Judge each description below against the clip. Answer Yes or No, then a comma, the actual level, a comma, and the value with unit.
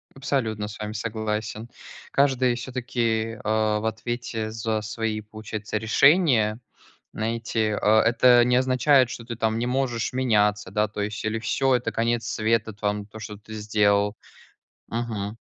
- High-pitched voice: No, low, 110 Hz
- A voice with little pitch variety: Yes, narrow, 2.0 semitones